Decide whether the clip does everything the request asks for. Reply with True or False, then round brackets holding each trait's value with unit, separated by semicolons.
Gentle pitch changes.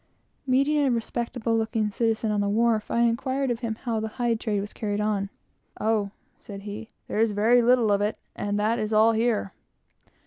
True (2.1 semitones)